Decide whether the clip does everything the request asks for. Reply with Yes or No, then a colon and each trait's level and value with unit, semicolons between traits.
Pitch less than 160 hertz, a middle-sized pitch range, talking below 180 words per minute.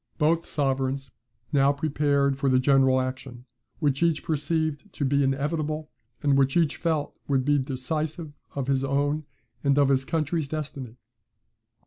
No: medium, 140 Hz; narrow, 2.2 semitones; average, 145 wpm